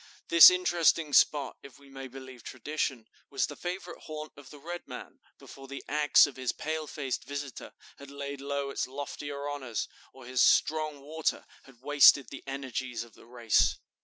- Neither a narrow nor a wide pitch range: No, narrow, 2.3 semitones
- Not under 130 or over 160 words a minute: No, average, 175 wpm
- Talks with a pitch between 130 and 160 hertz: Yes, medium, 140 Hz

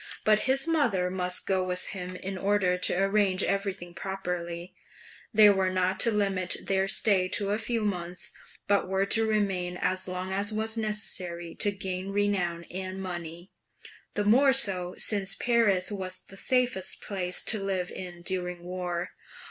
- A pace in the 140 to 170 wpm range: Yes, average, 160 wpm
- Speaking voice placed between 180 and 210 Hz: Yes, high, 190 Hz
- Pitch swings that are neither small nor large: No, narrow, 2.2 semitones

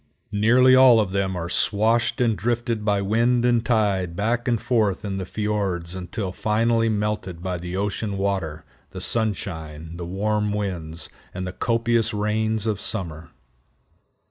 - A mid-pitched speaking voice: No, low, 105 Hz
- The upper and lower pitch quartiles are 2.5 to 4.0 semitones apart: Yes, average, 3.4 semitones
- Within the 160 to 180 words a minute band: No, average, 150 wpm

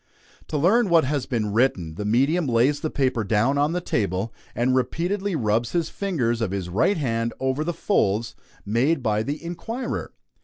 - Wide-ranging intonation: Yes, wide, 6.5 semitones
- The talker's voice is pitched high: No, low, 130 Hz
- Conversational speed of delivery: Yes, average, 180 wpm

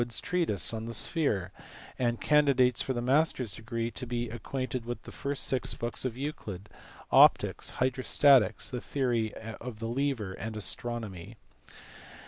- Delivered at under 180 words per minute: Yes, average, 150 wpm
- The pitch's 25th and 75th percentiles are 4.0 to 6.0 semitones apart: No, average, 2.8 semitones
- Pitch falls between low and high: No, low, 120 Hz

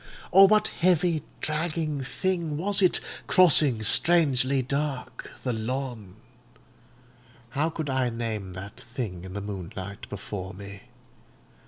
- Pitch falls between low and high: No, low, 130 Hz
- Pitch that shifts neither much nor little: No, wide, 7.4 semitones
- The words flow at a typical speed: No, slow, 120 wpm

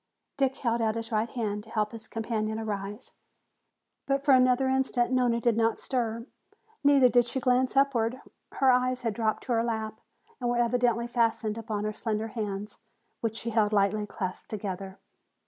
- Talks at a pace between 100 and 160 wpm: No, average, 175 wpm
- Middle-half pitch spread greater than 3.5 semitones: No, narrow, 2.5 semitones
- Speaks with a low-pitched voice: No, high, 230 Hz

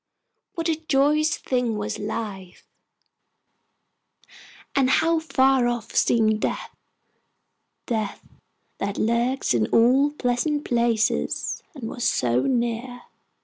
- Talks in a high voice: Yes, high, 240 Hz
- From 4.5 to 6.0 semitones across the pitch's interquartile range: No, average, 3.7 semitones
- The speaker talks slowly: Yes, slow, 105 wpm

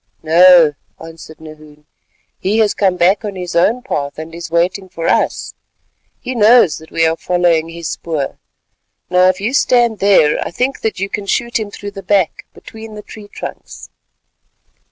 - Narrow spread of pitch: No, average, 4.2 semitones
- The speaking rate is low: No, average, 175 wpm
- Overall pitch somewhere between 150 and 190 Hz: Yes, medium, 185 Hz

